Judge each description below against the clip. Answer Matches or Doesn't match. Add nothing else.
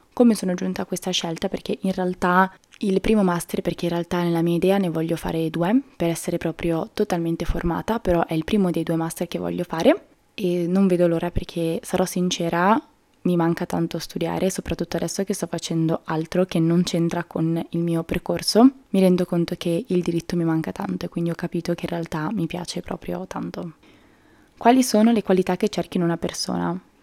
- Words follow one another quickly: Matches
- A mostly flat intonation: Matches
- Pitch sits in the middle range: Matches